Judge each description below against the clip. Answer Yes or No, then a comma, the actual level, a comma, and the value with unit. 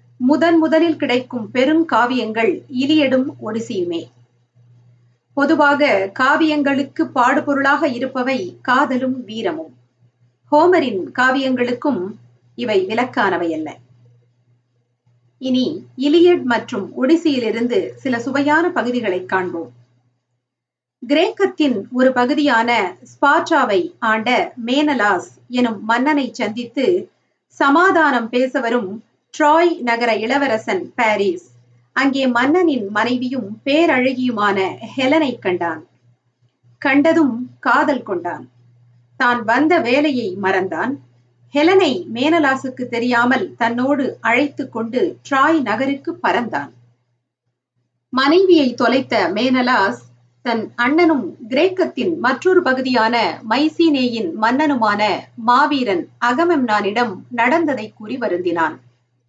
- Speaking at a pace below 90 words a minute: Yes, average, 80 wpm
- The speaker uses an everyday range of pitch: No, wide, 7.5 semitones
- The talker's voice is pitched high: Yes, high, 245 Hz